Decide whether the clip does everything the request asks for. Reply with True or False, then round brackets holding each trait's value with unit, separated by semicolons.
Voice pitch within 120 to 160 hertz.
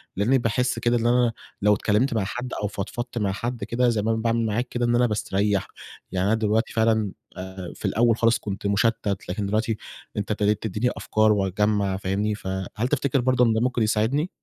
False (110 Hz)